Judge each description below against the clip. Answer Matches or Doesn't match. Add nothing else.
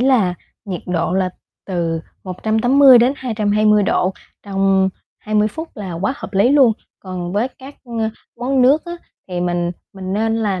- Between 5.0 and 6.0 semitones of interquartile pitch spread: Doesn't match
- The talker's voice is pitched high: Matches